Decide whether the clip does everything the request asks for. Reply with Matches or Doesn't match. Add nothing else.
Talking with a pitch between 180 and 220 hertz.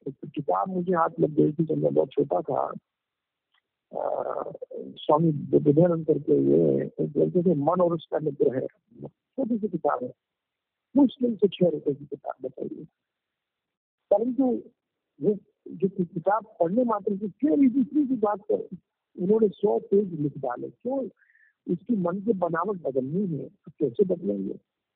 Matches